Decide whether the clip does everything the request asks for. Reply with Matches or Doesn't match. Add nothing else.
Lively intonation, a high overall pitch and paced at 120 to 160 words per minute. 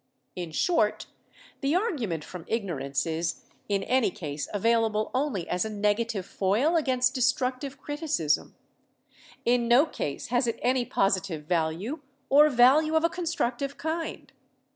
Matches